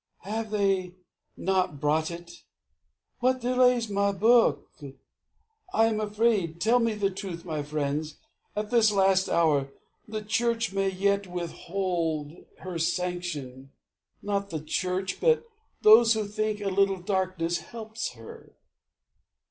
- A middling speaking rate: No, slow, 125 wpm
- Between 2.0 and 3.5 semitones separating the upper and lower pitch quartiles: No, average, 4.1 semitones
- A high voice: Yes, high, 195 Hz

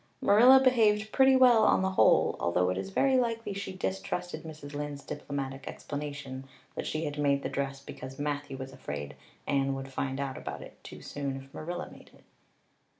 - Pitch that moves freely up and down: Yes, wide, 6.1 semitones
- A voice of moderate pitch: Yes, medium, 145 Hz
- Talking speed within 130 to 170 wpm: No, average, 185 wpm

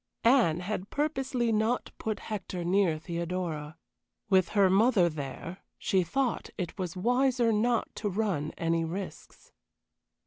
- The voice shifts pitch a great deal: No, average, 5.0 semitones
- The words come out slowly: Yes, slow, 130 wpm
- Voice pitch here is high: Yes, high, 195 Hz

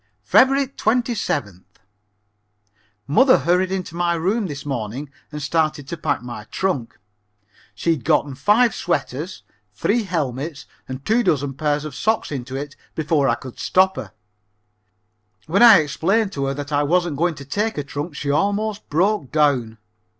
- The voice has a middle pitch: Yes, medium, 155 Hz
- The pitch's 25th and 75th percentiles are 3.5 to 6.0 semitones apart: Yes, wide, 5.5 semitones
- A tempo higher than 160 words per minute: No, average, 155 wpm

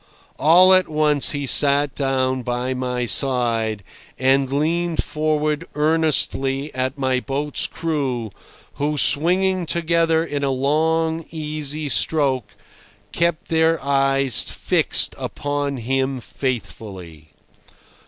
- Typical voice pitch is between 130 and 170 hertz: Yes, medium, 140 Hz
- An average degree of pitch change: Yes, average, 3.3 semitones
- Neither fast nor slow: No, slow, 105 wpm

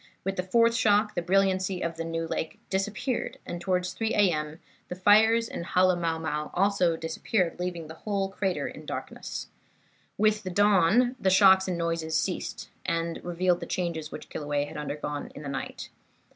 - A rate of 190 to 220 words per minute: No, average, 170 wpm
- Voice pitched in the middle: Yes, medium, 180 Hz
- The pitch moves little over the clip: No, average, 3.0 semitones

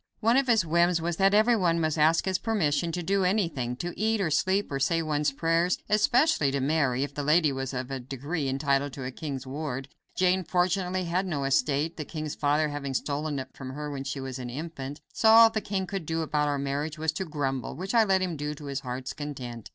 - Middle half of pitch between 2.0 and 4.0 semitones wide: No, average, 4.7 semitones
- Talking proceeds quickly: Yes, fast, 235 wpm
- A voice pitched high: No, medium, 155 Hz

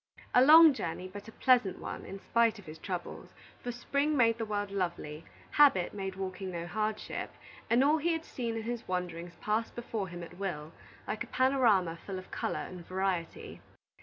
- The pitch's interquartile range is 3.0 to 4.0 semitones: No, average, 4.9 semitones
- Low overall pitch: No, high, 205 Hz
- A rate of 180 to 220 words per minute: Yes, average, 190 wpm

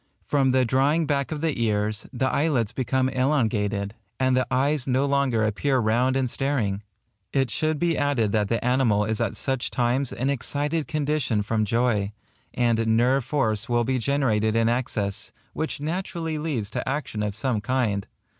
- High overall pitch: No, low, 125 Hz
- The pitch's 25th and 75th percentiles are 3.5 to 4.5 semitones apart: Yes, average, 4.2 semitones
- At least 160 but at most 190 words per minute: Yes, average, 175 wpm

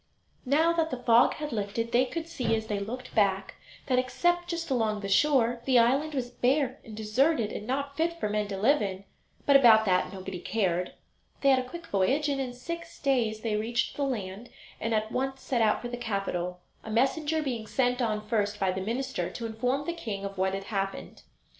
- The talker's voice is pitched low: No, high, 240 Hz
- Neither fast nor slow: No, fast, 210 wpm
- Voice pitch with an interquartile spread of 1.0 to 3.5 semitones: No, average, 4.5 semitones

